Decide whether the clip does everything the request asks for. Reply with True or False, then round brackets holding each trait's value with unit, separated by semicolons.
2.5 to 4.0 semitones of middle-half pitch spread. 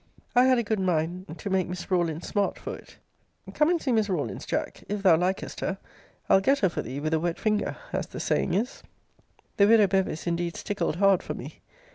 True (3.4 semitones)